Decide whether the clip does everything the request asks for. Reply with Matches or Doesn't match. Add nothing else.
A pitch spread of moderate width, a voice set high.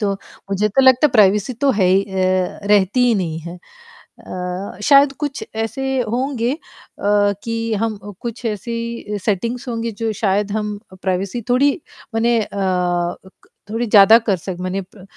Matches